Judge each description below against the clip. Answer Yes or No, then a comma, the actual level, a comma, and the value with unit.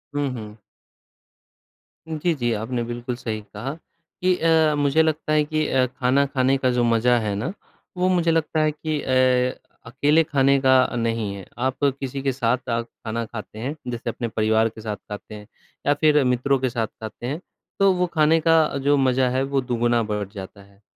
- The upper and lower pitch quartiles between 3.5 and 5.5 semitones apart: Yes, average, 4.1 semitones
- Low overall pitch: Yes, low, 130 Hz